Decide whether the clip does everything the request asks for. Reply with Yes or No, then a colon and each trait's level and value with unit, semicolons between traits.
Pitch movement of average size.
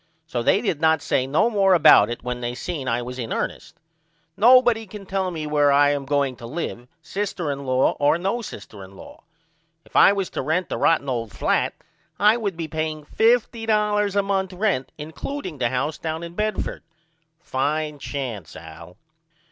No: wide, 7.0 semitones